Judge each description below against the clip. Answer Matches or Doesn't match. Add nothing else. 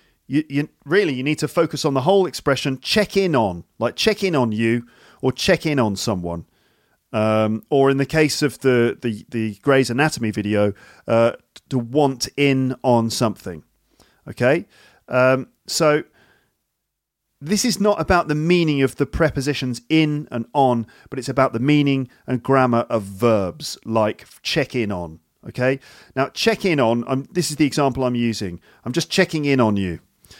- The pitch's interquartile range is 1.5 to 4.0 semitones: Doesn't match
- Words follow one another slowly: Doesn't match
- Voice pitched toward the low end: Matches